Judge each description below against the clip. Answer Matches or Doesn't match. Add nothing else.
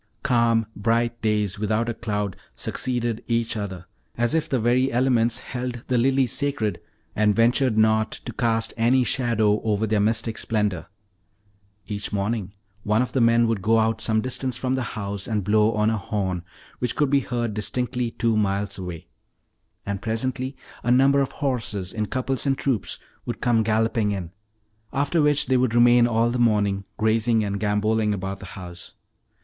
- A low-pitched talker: Matches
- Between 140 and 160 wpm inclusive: Doesn't match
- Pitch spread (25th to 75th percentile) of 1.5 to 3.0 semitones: Matches